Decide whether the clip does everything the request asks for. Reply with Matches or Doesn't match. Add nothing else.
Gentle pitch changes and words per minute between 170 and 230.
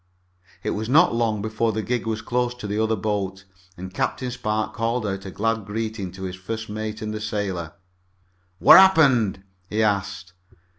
Matches